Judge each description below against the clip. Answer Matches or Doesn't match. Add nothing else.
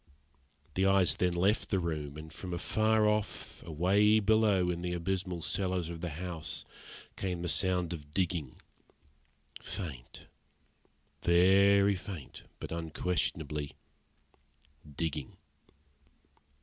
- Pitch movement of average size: Matches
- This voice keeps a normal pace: Doesn't match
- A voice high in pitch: Doesn't match